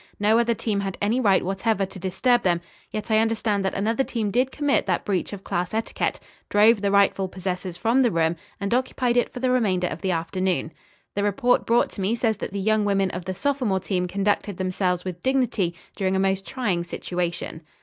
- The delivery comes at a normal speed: No, fast, 210 wpm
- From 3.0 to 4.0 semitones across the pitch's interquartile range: Yes, average, 3.5 semitones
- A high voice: Yes, high, 200 Hz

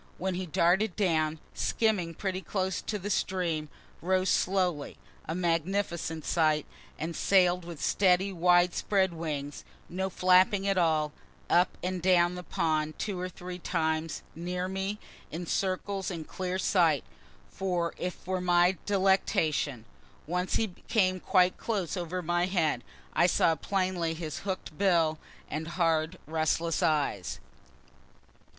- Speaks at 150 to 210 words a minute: No, slow, 135 wpm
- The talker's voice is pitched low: No, medium, 180 Hz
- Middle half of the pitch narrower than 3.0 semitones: Yes, narrow, 2.5 semitones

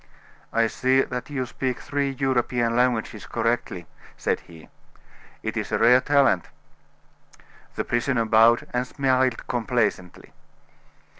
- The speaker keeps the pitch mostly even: Yes, narrow, 2.2 semitones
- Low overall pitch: Yes, low, 125 Hz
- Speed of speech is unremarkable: No, slow, 120 wpm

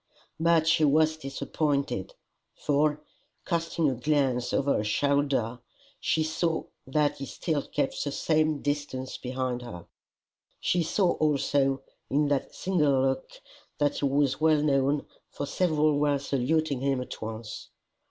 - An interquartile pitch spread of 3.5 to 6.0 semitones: No, narrow, 2.5 semitones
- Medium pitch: Yes, medium, 145 Hz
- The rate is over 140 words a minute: No, slow, 135 wpm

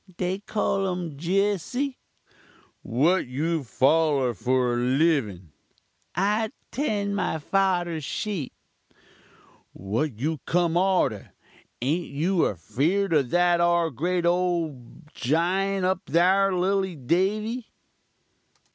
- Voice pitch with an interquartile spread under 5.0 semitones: No, wide, 5.4 semitones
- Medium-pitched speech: Yes, medium, 170 Hz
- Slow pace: Yes, slow, 100 wpm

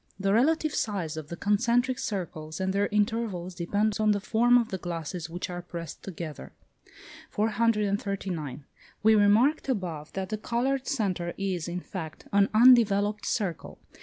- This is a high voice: Yes, high, 200 Hz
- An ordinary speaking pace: Yes, average, 150 wpm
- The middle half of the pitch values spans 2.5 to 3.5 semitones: No, average, 4.0 semitones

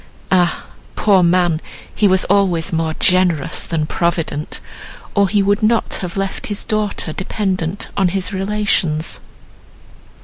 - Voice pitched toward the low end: No, medium, 185 Hz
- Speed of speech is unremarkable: No, slow, 130 wpm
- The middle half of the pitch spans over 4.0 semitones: No, average, 3.0 semitones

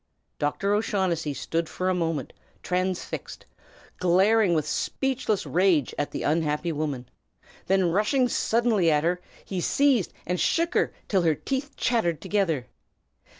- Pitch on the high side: No, medium, 180 Hz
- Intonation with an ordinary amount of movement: Yes, average, 4.5 semitones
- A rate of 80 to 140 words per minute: Yes, slow, 135 wpm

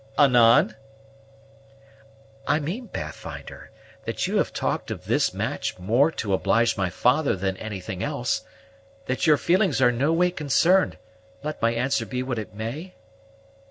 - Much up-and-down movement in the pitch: Yes, wide, 5.9 semitones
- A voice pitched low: Yes, low, 125 Hz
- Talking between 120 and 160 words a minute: Yes, average, 145 wpm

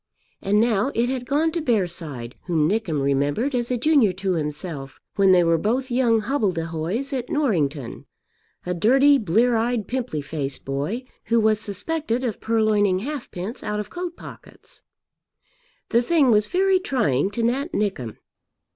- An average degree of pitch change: No, wide, 7.0 semitones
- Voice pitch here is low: No, high, 215 Hz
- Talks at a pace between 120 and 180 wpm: Yes, average, 155 wpm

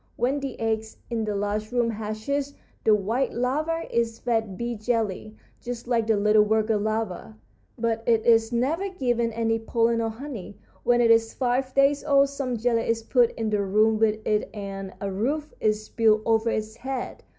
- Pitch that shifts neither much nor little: No, narrow, 2.3 semitones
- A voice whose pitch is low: No, high, 225 Hz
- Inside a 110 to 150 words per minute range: No, average, 185 wpm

